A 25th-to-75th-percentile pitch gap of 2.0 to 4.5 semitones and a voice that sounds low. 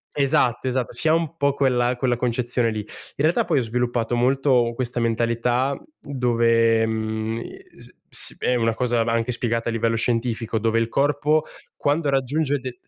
Yes: average, 2.7 semitones; low, 120 Hz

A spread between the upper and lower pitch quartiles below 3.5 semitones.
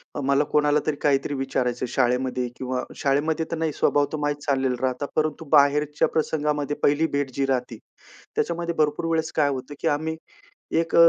Yes: average, 2.7 semitones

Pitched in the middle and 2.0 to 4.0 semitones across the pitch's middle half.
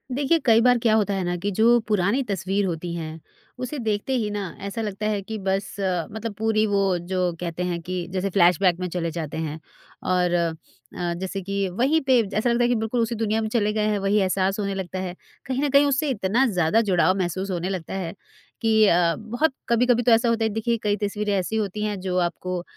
No: high, 200 Hz; average, 3.5 semitones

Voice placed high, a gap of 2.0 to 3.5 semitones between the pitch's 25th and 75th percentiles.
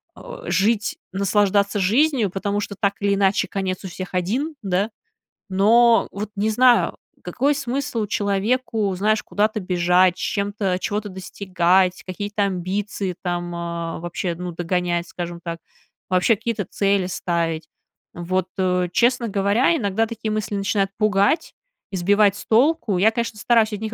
Yes: high, 200 Hz; average, 3.0 semitones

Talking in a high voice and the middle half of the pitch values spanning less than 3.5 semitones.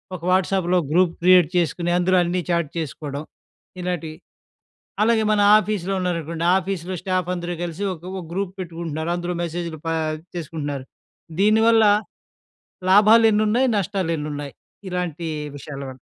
No: medium, 175 Hz; average, 2.7 semitones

